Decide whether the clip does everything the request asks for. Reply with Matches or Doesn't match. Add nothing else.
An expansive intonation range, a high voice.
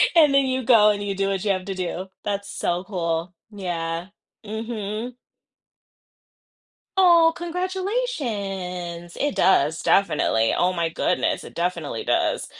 Matches